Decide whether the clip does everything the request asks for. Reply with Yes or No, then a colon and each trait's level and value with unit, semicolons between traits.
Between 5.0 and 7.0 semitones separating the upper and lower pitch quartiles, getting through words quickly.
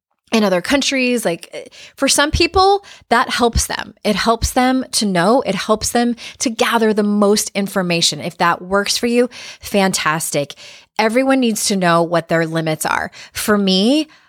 No: wide, 5.4 semitones; average, 165 wpm